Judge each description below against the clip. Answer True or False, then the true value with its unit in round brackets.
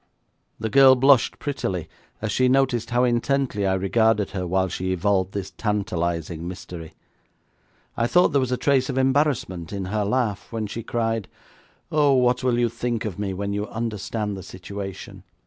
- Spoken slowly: False (170 wpm)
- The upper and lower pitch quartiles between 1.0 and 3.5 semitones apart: False (4.7 semitones)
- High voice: False (110 Hz)